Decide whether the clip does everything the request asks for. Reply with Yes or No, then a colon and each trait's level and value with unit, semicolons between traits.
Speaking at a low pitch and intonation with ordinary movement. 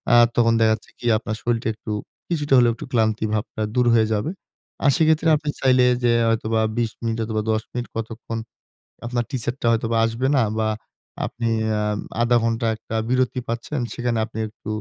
No: low, 115 Hz; narrow, 1.9 semitones